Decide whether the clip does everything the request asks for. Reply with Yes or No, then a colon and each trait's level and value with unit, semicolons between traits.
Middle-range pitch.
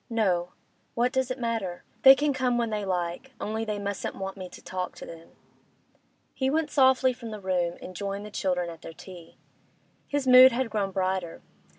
No: high, 210 Hz